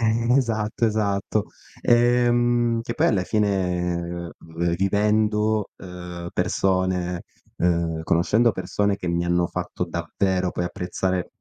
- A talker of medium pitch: No, very low, 95 Hz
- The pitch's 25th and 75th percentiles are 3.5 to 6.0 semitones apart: Yes, average, 3.8 semitones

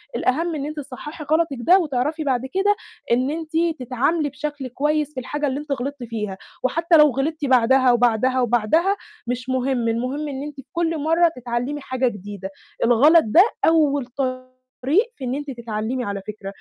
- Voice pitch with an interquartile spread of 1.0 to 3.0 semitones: No, average, 3.6 semitones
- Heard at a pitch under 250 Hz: No, very high, 265 Hz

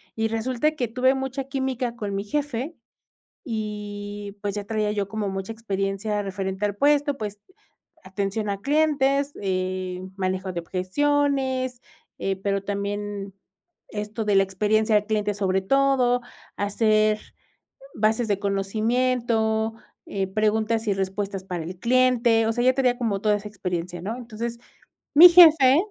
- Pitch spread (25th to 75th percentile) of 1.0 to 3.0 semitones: No, average, 3.9 semitones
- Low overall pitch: No, high, 215 Hz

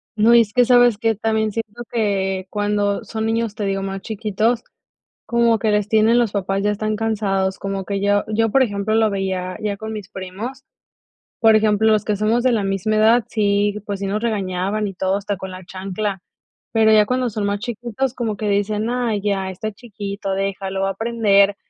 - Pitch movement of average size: No, narrow, 2.1 semitones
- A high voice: Yes, high, 210 Hz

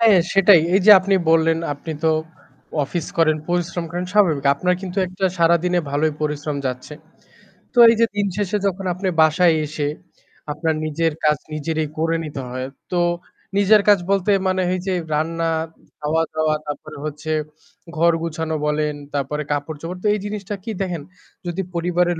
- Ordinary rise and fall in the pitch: Yes, average, 3.3 semitones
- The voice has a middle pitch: Yes, medium, 165 Hz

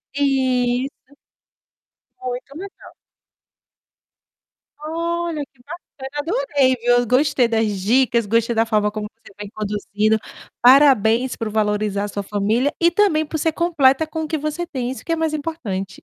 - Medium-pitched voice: No, very high, 260 Hz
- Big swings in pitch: Yes, wide, 5.7 semitones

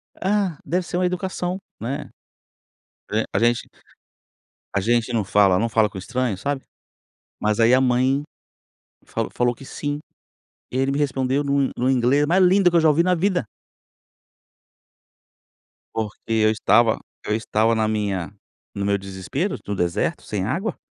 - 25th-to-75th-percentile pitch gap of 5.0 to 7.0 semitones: Yes, wide, 5.6 semitones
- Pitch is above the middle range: No, low, 125 Hz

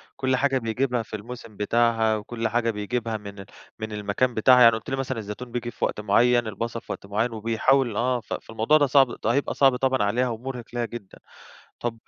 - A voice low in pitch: Yes, low, 115 Hz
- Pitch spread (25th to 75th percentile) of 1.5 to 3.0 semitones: Yes, narrow, 2.4 semitones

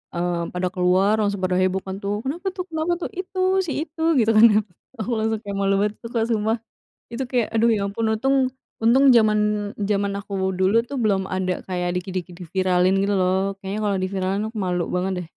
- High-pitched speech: Yes, high, 200 Hz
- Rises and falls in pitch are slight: No, average, 3.2 semitones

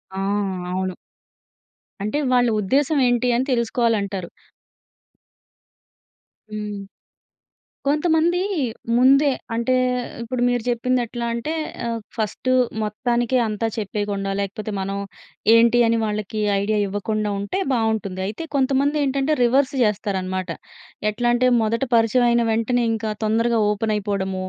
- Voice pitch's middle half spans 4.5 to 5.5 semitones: No, average, 3.3 semitones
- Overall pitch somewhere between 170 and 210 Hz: No, high, 230 Hz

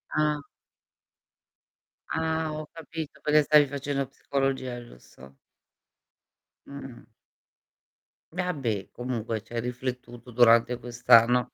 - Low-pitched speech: Yes, low, 125 Hz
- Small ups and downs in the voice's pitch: No, average, 3.8 semitones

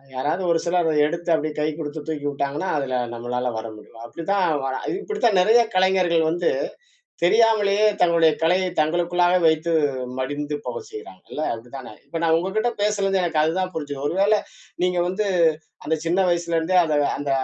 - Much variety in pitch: No, average, 4.0 semitones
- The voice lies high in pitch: No, medium, 170 Hz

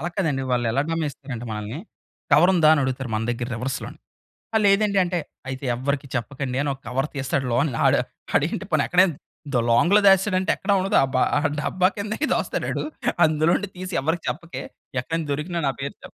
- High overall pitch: No, medium, 145 Hz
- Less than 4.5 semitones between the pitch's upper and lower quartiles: No, wide, 5.4 semitones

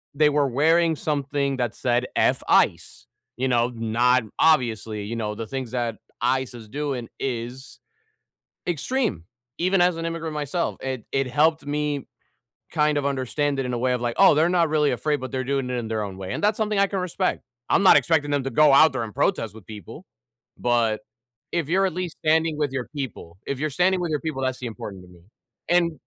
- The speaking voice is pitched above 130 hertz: Yes, medium, 140 Hz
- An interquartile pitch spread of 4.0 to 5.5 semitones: Yes, average, 4.8 semitones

